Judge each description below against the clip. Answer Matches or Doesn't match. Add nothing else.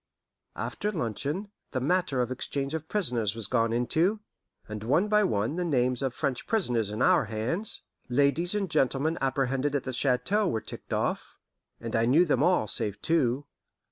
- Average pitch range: Doesn't match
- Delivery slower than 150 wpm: Doesn't match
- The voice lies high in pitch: Doesn't match